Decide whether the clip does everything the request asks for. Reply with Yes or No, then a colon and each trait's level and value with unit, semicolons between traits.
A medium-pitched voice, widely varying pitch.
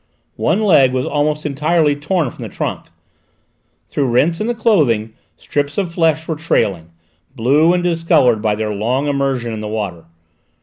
Yes: medium, 145 Hz; wide, 6.1 semitones